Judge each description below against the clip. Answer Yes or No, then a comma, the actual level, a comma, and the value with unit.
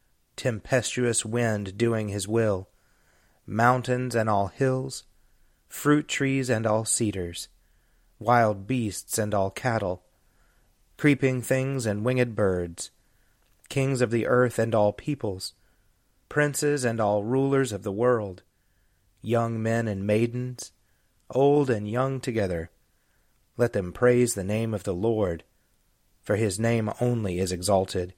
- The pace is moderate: No, slow, 130 wpm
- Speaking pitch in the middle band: No, low, 110 Hz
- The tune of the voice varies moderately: Yes, average, 4.1 semitones